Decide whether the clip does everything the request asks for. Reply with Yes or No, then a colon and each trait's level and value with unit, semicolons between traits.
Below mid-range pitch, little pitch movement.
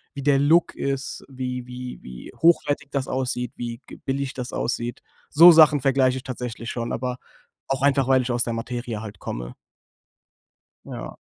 Yes: low, 130 Hz; narrow, 2.3 semitones